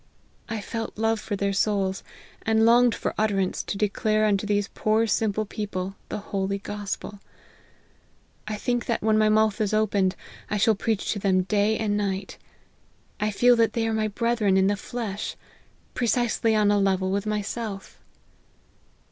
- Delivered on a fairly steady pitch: Yes, narrow, 1.8 semitones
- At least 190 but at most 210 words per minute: No, average, 170 wpm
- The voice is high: Yes, high, 210 Hz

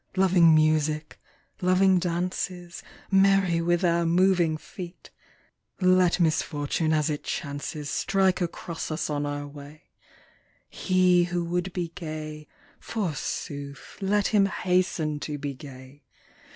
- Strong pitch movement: No, average, 3.2 semitones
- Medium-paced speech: No, slow, 115 wpm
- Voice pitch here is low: No, medium, 170 Hz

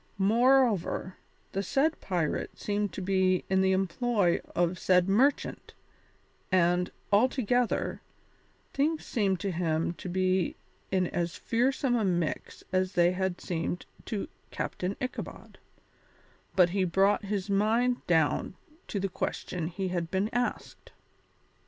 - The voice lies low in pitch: No, high, 190 Hz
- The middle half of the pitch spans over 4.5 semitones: No, average, 3.4 semitones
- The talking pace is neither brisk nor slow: No, slow, 125 wpm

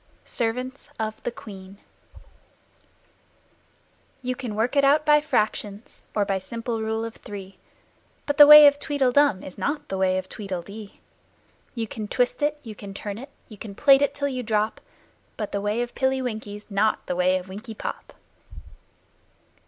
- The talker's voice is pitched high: Yes, high, 220 Hz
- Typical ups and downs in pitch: Yes, average, 4.9 semitones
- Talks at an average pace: Yes, average, 170 wpm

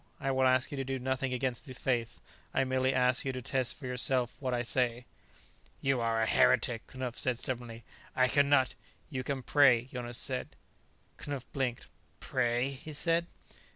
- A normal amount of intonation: No, narrow, 1.5 semitones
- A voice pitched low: Yes, low, 130 Hz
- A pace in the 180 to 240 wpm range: Yes, average, 190 wpm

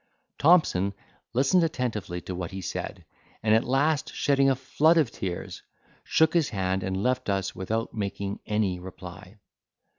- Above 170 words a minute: No, average, 150 wpm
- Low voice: Yes, low, 105 Hz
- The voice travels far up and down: Yes, wide, 6.3 semitones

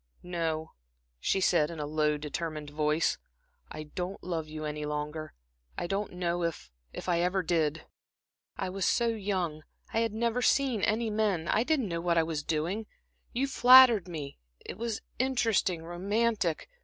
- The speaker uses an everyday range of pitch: No, wide, 5.7 semitones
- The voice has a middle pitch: Yes, medium, 175 Hz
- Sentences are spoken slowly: No, average, 160 wpm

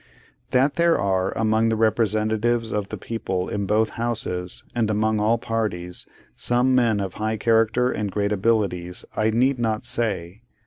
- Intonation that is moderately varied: No, narrow, 2.3 semitones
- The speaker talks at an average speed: Yes, average, 160 wpm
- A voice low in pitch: Yes, low, 110 Hz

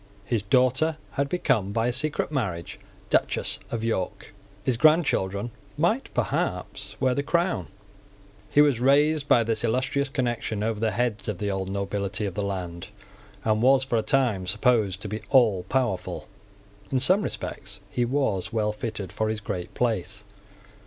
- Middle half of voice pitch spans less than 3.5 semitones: No, average, 4.8 semitones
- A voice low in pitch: Yes, low, 115 Hz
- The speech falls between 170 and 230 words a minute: No, average, 160 wpm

